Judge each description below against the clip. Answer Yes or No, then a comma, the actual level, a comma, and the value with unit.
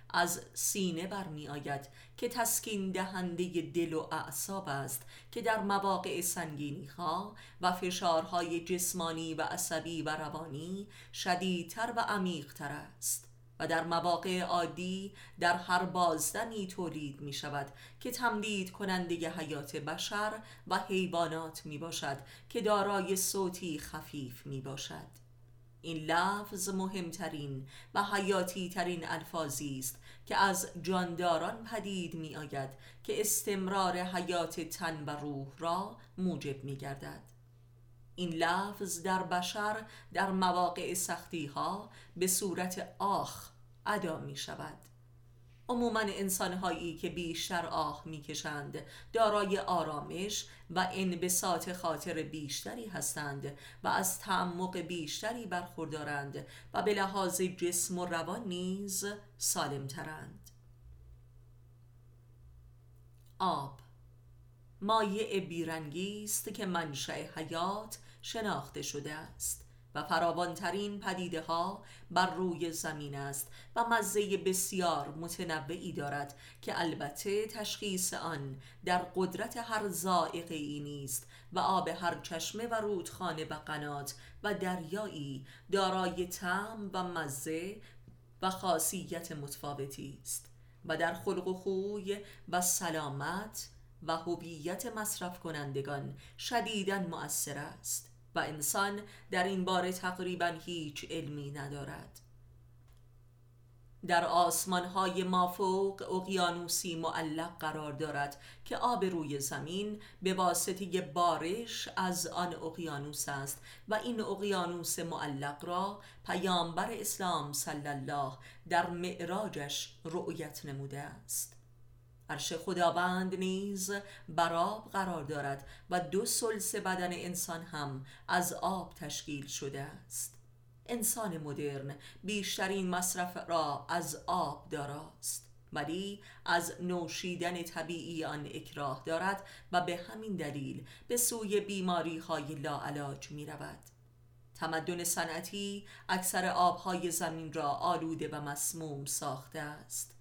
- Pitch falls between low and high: Yes, medium, 170 Hz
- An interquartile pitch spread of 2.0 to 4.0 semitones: No, average, 4.6 semitones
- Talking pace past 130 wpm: No, average, 110 wpm